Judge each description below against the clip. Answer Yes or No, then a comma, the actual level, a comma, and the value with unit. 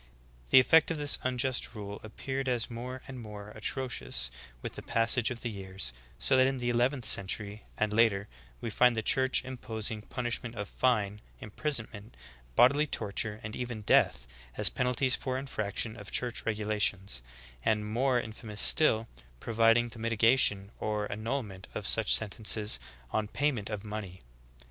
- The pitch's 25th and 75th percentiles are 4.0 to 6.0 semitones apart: No, average, 3.2 semitones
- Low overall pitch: Yes, low, 115 Hz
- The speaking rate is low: No, average, 165 wpm